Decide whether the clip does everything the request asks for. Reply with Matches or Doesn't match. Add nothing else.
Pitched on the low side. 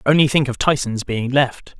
Matches